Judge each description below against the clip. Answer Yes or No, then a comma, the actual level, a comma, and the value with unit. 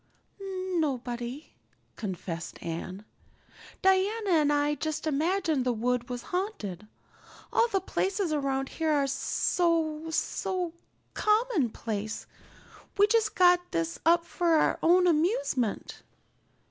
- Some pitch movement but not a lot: No, wide, 6.9 semitones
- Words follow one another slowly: Yes, slow, 110 wpm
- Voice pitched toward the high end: Yes, very high, 315 Hz